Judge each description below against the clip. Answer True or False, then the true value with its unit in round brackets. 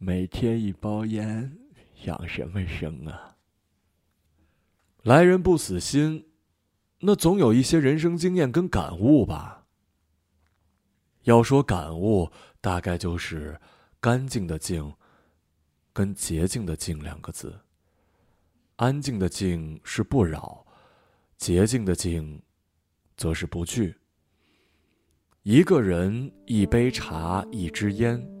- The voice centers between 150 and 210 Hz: False (90 Hz)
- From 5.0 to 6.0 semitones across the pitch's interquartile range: True (5.6 semitones)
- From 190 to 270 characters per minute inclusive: False (150 characters per minute)